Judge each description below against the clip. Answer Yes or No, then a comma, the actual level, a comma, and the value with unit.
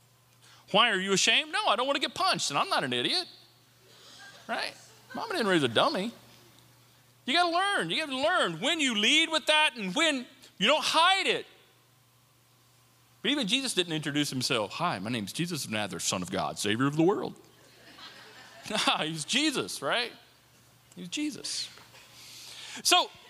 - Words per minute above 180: No, average, 175 wpm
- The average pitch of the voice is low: No, high, 225 Hz